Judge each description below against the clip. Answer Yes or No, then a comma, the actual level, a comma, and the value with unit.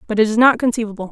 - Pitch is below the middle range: No, high, 225 Hz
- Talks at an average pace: No, fast, 270 wpm